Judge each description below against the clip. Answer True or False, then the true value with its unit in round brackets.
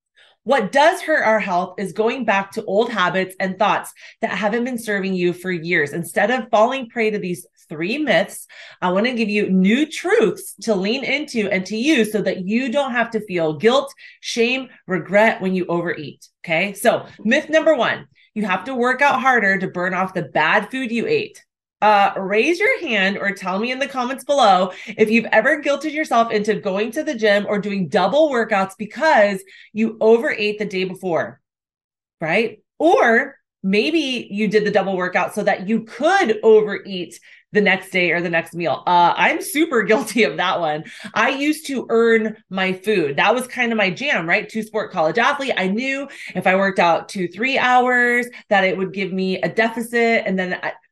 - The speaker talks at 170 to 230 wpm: True (195 wpm)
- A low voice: False (215 Hz)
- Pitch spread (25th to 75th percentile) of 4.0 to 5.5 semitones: True (4.5 semitones)